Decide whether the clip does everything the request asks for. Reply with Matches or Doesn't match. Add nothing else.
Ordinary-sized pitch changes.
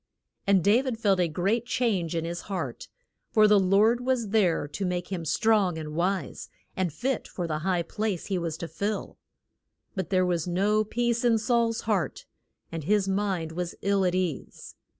Matches